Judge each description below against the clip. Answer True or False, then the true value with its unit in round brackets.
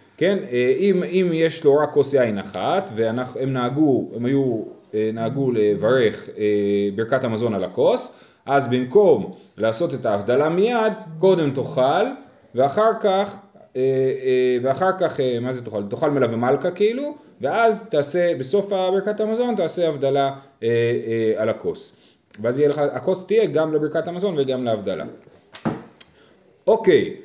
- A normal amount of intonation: False (7.3 semitones)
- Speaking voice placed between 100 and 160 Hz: True (140 Hz)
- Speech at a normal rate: True (120 wpm)